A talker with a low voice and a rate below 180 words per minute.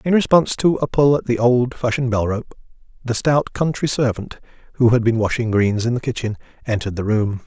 No: low, 120 Hz; average, 200 wpm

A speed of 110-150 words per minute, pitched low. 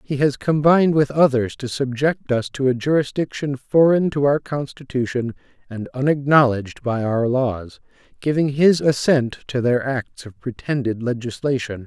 Yes: average, 145 wpm; low, 130 Hz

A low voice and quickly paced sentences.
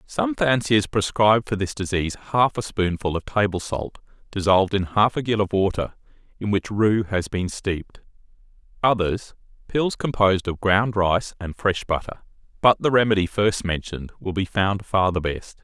No: low, 100 Hz; average, 175 wpm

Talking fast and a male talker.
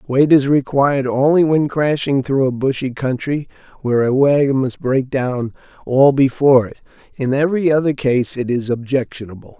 No: average, 165 wpm; male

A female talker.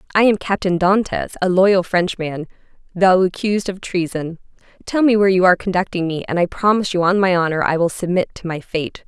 Yes: female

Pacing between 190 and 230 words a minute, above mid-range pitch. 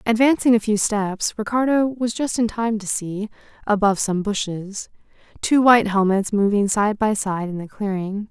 No: average, 175 wpm; high, 210 Hz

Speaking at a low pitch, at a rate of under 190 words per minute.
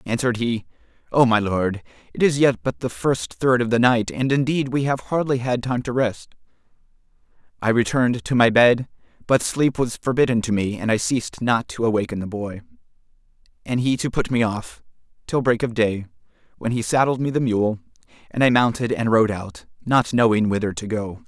No: low, 115 Hz; average, 195 wpm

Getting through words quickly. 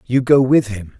Yes: fast, 240 wpm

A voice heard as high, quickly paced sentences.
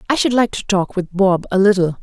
Yes: high, 195 Hz; fast, 265 wpm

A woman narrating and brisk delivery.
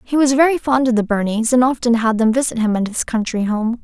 Yes: female; fast, 265 wpm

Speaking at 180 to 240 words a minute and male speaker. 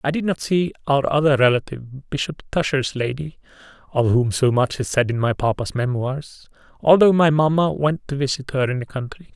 Yes: average, 185 wpm; male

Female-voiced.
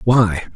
No: male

